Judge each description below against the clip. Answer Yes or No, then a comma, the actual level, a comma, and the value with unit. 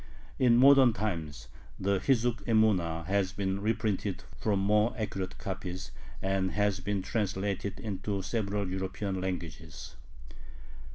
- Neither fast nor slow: No, slow, 115 wpm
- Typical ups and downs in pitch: No, narrow, 2.3 semitones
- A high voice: No, low, 100 Hz